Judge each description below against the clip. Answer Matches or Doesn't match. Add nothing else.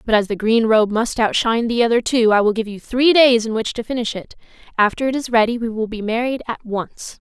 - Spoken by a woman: Matches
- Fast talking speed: Matches